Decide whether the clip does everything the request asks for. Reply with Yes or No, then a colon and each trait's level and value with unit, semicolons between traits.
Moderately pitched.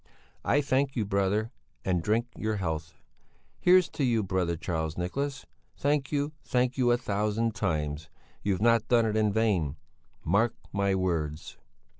No: low, 105 Hz